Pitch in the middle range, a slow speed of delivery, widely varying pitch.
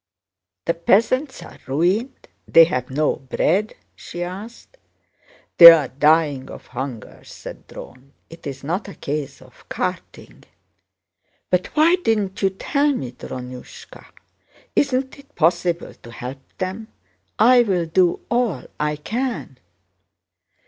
Yes: medium, 170 Hz; slow, 115 wpm; wide, 8.1 semitones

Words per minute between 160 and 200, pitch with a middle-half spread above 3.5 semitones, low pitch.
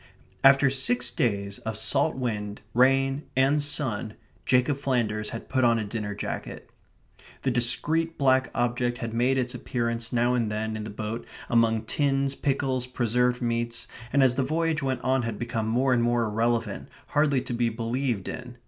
No: average, 170 wpm; average, 2.7 semitones; low, 120 Hz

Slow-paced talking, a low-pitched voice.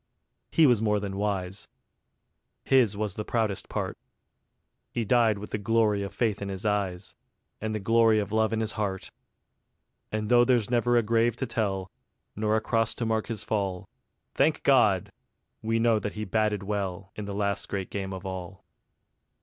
No: average, 180 wpm; low, 105 Hz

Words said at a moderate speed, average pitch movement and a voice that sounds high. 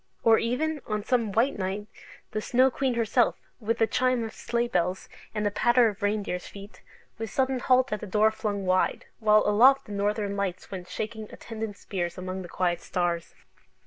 Yes: average, 185 wpm; average, 3.1 semitones; high, 215 Hz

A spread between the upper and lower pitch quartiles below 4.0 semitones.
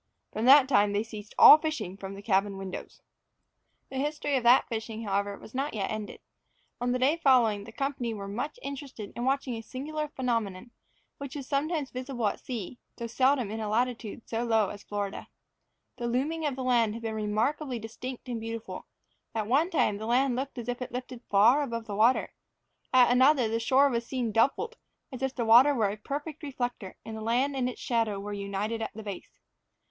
Yes: average, 3.6 semitones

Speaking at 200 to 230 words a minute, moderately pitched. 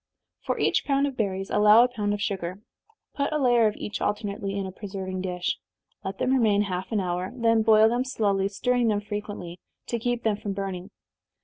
No: fast, 205 wpm; high, 205 Hz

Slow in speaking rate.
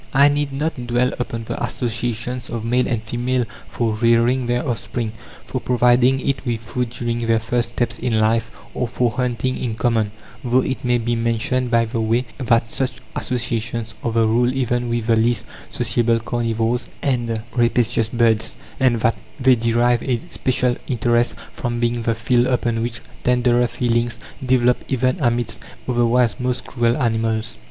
No: average, 165 wpm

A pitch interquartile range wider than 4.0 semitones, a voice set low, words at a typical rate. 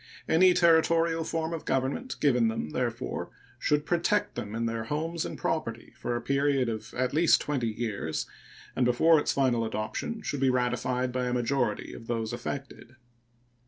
Yes: wide, 5.4 semitones; low, 130 Hz; average, 165 wpm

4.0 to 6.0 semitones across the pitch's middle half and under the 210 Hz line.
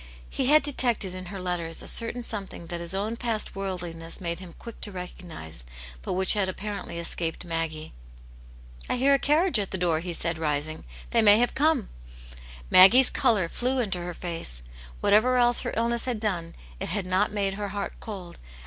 Yes: average, 5.2 semitones; high, 190 Hz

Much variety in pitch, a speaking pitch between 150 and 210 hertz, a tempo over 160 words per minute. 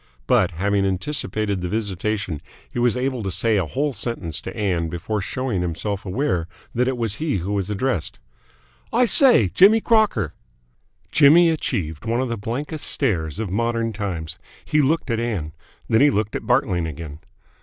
No: wide, 5.9 semitones; low, 110 Hz; average, 170 wpm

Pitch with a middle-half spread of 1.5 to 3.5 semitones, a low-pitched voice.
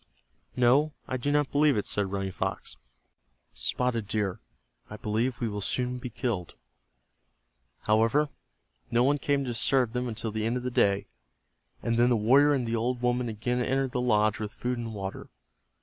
Yes: average, 2.8 semitones; low, 120 Hz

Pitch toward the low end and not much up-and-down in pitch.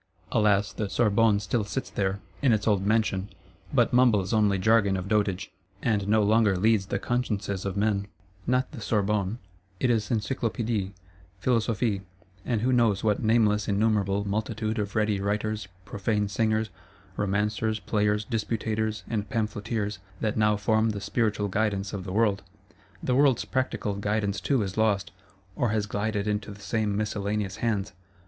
Yes: low, 105 Hz; narrow, 1.7 semitones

